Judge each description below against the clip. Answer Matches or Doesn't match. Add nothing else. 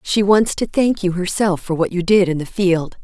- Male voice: Doesn't match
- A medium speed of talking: Doesn't match